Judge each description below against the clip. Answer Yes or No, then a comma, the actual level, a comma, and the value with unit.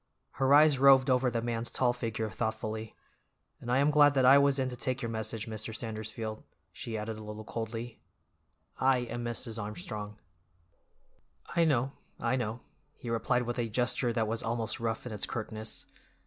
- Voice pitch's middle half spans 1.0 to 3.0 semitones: Yes, narrow, 2.6 semitones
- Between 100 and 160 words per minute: No, average, 175 wpm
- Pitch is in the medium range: No, low, 115 Hz